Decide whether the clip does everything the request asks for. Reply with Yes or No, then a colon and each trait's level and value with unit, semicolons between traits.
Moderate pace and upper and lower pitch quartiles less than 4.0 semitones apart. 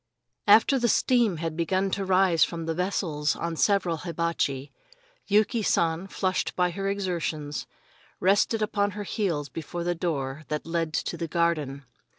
Yes: average, 155 wpm; average, 3.5 semitones